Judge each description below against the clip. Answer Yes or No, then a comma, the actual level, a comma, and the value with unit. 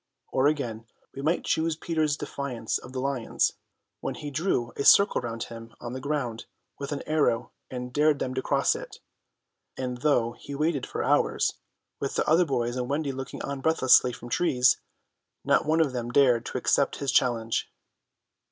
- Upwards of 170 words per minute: Yes, average, 180 wpm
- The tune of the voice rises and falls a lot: No, average, 3.3 semitones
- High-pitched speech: No, low, 135 Hz